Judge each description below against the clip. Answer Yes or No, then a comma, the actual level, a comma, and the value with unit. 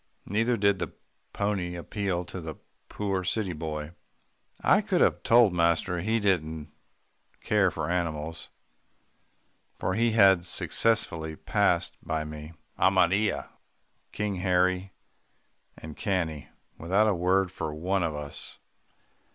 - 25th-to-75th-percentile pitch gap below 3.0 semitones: No, average, 3.7 semitones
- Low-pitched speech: Yes, very low, 90 Hz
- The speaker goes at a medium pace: No, slow, 120 wpm